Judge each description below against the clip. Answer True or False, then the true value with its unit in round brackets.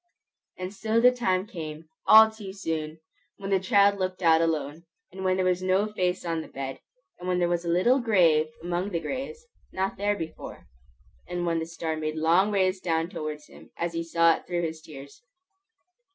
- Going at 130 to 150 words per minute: False (195 wpm)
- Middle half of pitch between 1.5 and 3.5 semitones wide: True (3.2 semitones)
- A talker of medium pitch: True (180 Hz)